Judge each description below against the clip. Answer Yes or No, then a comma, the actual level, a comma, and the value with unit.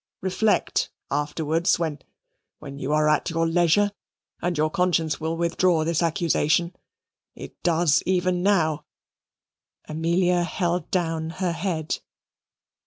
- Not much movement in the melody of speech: Yes, narrow, 2.2 semitones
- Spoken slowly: Yes, slow, 110 wpm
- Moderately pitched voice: Yes, medium, 165 Hz